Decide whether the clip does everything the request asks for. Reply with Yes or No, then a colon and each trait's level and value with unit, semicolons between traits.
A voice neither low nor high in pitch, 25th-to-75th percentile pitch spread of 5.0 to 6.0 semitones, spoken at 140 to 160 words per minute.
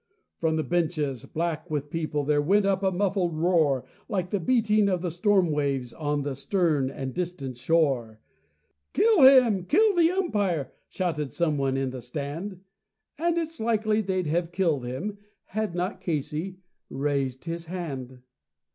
Yes: medium, 170 Hz; wide, 5.5 semitones; average, 155 wpm